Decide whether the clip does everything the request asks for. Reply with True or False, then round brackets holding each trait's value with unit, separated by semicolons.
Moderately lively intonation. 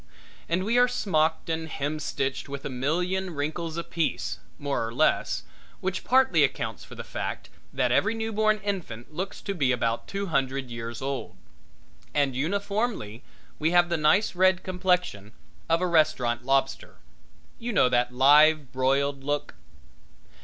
False (5.8 semitones)